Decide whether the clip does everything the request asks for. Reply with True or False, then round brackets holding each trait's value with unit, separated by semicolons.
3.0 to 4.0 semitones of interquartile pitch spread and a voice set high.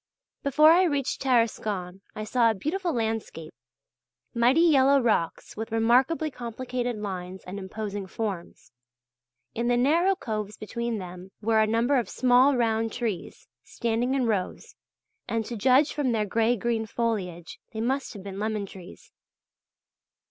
True (3.5 semitones; 230 Hz)